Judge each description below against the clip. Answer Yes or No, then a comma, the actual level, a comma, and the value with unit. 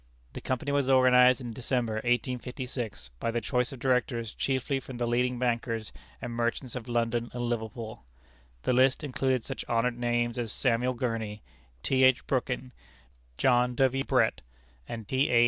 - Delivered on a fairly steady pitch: Yes, narrow, 1.6 semitones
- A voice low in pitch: Yes, low, 125 Hz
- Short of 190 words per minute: Yes, average, 160 wpm